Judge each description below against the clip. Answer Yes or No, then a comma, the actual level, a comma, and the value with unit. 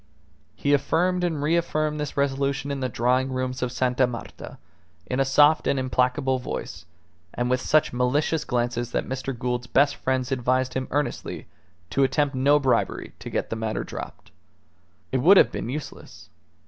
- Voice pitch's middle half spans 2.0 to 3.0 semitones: Yes, narrow, 2.5 semitones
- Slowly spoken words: No, average, 165 wpm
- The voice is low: Yes, low, 130 Hz